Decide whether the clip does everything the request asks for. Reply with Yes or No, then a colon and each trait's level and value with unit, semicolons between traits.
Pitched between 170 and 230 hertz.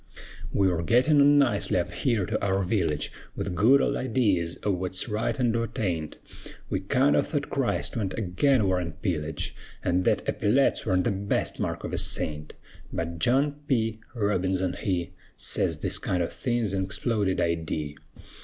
No: low, 100 Hz